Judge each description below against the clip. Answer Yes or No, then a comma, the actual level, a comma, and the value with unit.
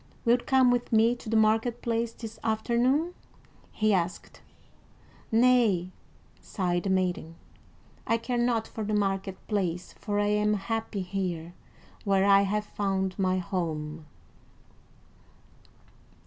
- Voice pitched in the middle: No, high, 210 Hz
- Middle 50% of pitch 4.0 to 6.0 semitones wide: No, average, 3.5 semitones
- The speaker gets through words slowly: Yes, slow, 125 wpm